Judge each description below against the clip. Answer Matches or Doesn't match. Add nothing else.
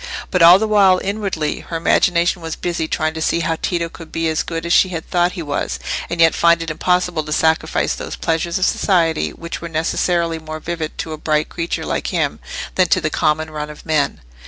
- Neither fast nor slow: Doesn't match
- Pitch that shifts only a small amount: Matches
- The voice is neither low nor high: Matches